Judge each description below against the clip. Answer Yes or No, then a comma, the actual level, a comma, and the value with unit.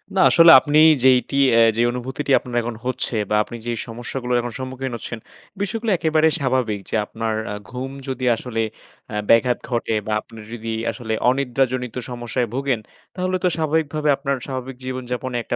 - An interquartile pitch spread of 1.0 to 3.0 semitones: Yes, narrow, 2.5 semitones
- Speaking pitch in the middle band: No, low, 130 Hz